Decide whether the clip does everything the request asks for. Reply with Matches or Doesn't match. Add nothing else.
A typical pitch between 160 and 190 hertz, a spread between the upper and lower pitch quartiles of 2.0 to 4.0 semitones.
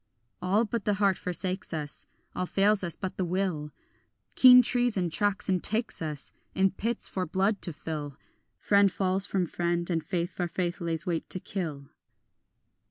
Matches